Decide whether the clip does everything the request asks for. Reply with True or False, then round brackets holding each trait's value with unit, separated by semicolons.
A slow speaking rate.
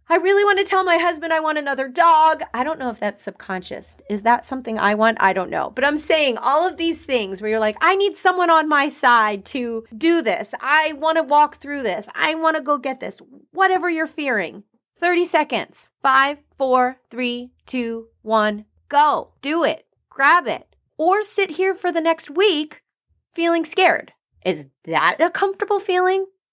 False (190 wpm)